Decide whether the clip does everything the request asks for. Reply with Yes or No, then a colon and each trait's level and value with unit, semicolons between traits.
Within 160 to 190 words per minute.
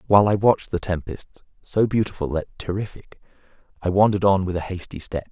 Yes: average, 180 wpm